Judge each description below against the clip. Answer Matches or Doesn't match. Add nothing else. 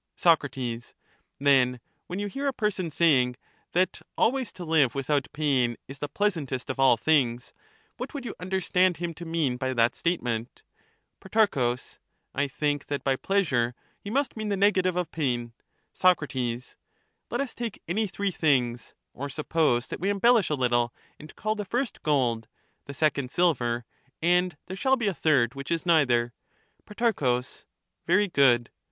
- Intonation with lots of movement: Matches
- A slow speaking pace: Doesn't match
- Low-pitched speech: Doesn't match